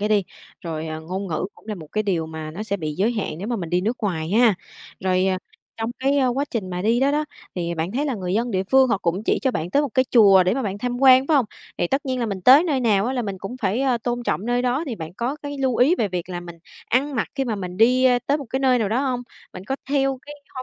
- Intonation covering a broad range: Yes, wide, 5.8 semitones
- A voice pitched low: No, high, 225 Hz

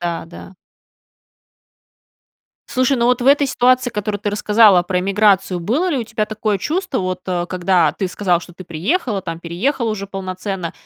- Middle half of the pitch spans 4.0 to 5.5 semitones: Yes, average, 4.8 semitones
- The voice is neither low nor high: No, high, 200 Hz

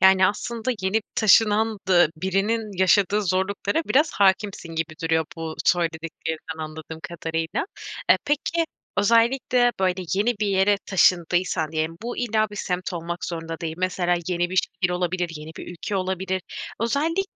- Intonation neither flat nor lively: Yes, average, 3.8 semitones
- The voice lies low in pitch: No, medium, 185 Hz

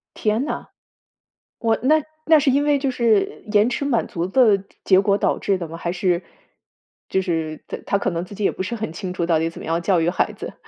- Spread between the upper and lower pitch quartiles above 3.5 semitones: Yes, wide, 5.5 semitones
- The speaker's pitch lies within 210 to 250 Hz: No, high, 195 Hz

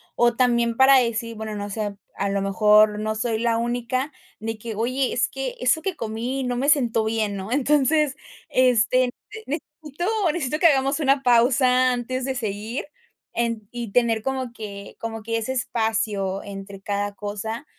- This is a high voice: Yes, high, 235 Hz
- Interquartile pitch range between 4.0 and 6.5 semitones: No, average, 3.2 semitones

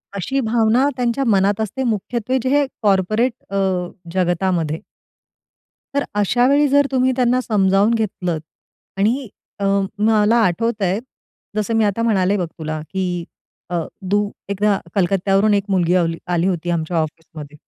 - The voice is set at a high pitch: Yes, high, 200 Hz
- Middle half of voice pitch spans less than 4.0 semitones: No, average, 4.4 semitones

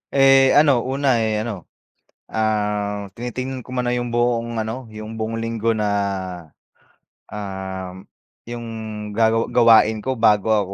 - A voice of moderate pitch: No, low, 115 Hz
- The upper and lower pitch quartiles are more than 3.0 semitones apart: No, narrow, 2.5 semitones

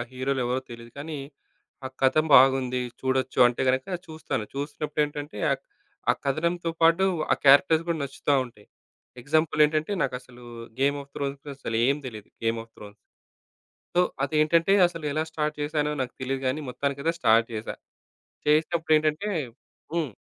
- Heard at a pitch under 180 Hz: Yes, medium, 140 Hz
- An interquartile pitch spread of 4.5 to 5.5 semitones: No, average, 3.3 semitones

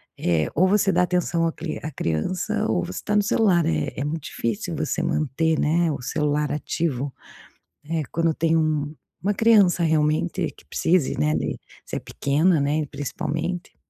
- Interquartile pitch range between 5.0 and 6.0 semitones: No, average, 3.5 semitones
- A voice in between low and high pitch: Yes, medium, 160 Hz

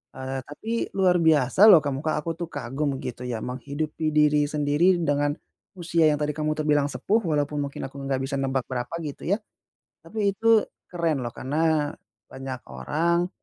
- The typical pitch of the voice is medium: Yes, medium, 150 Hz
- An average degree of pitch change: Yes, average, 3.4 semitones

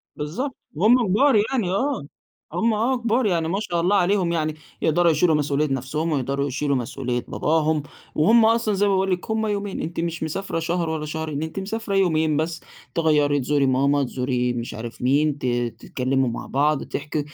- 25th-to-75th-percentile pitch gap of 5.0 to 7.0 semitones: Yes, average, 5.3 semitones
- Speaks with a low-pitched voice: No, medium, 160 Hz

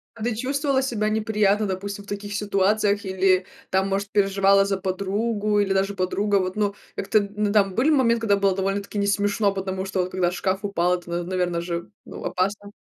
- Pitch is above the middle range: Yes, high, 200 Hz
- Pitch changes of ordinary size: No, narrow, 1.8 semitones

